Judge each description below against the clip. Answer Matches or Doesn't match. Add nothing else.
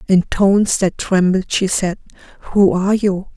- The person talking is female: Matches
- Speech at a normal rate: Matches